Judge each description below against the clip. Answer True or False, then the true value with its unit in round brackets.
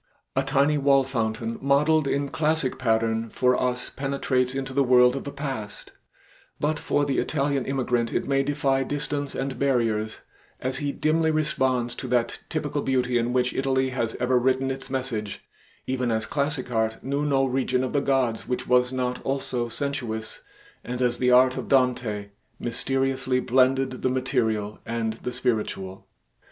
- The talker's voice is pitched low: True (130 Hz)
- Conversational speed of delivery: True (165 wpm)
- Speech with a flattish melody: True (2.1 semitones)